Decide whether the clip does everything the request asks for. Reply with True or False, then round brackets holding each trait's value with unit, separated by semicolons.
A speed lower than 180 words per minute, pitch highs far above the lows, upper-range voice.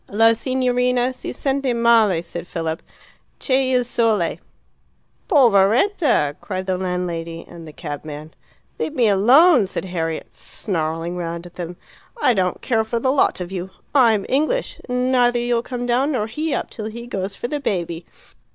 True (165 wpm; 6.1 semitones; 220 Hz)